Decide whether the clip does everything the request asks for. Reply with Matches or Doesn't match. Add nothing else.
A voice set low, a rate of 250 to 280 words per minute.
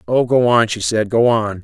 Matches